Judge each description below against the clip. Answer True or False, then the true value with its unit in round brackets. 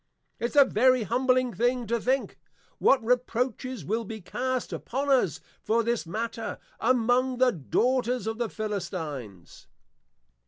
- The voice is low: False (235 Hz)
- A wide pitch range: False (2.8 semitones)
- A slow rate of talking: True (130 wpm)